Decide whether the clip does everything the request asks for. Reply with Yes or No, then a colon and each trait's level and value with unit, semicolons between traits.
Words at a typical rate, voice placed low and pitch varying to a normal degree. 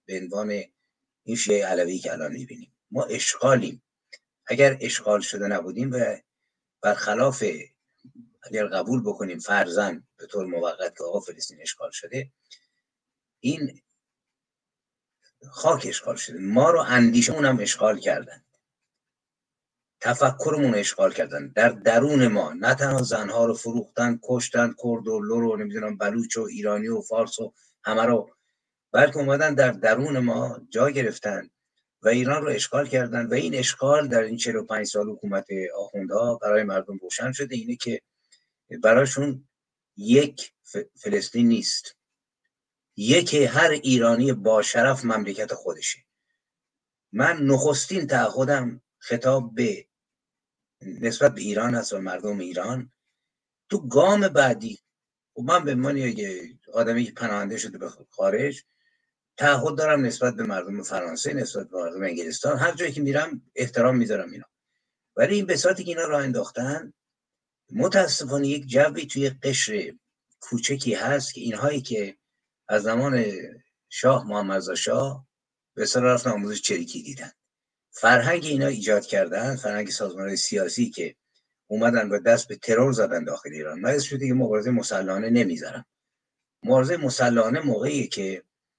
Yes: average, 135 wpm; low, 130 Hz; average, 4.3 semitones